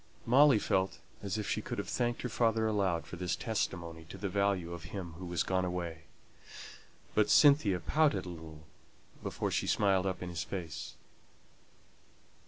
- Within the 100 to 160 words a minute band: No, average, 170 wpm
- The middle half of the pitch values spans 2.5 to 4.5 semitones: Yes, average, 3.6 semitones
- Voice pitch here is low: Yes, very low, 95 Hz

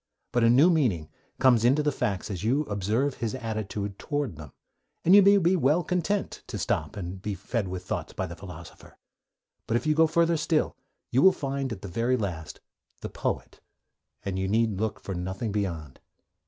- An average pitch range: No, wide, 7.2 semitones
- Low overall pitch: Yes, low, 115 Hz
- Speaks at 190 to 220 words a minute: Yes, average, 195 wpm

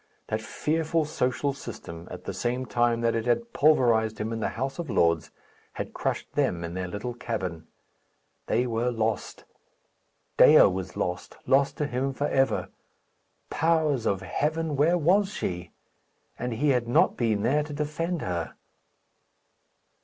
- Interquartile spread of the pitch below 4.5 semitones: No, wide, 5.5 semitones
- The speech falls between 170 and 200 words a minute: No, average, 155 wpm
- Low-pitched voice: Yes, low, 120 Hz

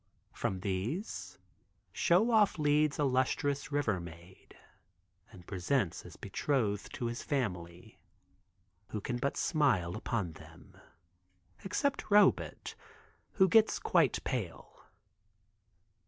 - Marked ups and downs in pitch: Yes, wide, 8.3 semitones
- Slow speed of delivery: Yes, slow, 105 wpm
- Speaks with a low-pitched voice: Yes, low, 130 Hz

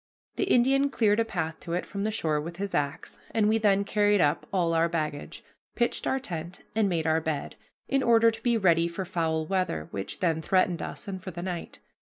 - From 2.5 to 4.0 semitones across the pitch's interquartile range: No, average, 4.8 semitones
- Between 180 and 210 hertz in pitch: Yes, medium, 185 Hz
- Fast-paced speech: Yes, fast, 220 wpm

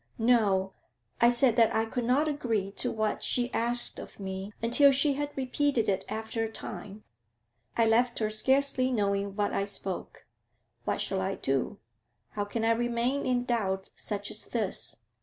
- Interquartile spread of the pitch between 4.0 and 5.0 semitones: No, average, 3.5 semitones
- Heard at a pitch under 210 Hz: No, high, 225 Hz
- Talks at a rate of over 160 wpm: Yes, average, 170 wpm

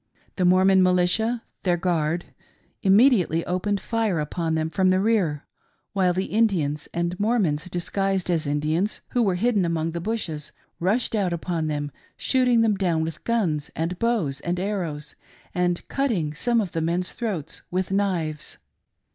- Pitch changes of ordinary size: Yes, average, 4.1 semitones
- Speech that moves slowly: No, average, 165 wpm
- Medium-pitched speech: Yes, medium, 180 Hz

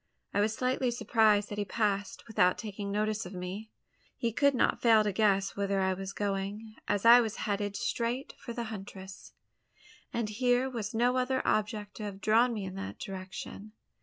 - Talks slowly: No, average, 185 wpm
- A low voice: No, high, 210 Hz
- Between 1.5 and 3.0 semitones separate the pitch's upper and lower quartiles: Yes, average, 2.7 semitones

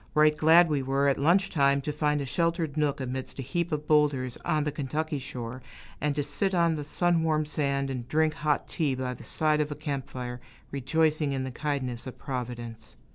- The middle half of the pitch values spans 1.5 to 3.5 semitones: Yes, average, 2.8 semitones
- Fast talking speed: Yes, fast, 210 wpm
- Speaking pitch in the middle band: Yes, medium, 145 Hz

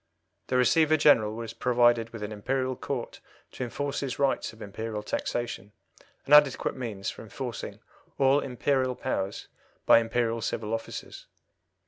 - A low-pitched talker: Yes, low, 120 Hz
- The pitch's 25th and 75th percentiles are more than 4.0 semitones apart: No, average, 3.2 semitones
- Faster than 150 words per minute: No, average, 140 wpm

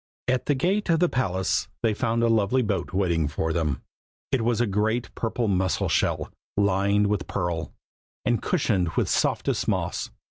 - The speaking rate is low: No, average, 170 wpm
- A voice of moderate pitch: No, low, 105 Hz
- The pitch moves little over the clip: No, average, 4.7 semitones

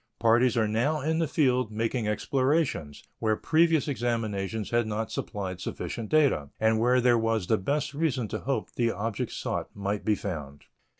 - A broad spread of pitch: No, average, 4.1 semitones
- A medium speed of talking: Yes, average, 170 wpm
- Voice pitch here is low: Yes, low, 115 Hz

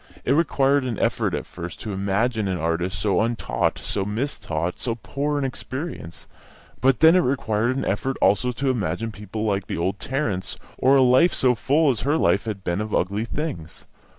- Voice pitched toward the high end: No, low, 115 Hz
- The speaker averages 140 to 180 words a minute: No, average, 190 wpm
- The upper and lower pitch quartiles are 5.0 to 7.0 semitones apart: Yes, wide, 5.6 semitones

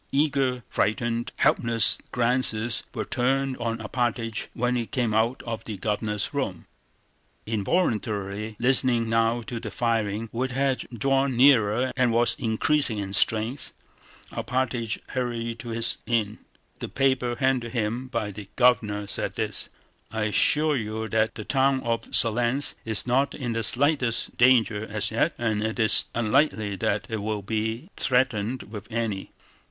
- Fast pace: No, average, 145 wpm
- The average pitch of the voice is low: Yes, low, 115 Hz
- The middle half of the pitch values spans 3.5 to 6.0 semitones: No, average, 2.7 semitones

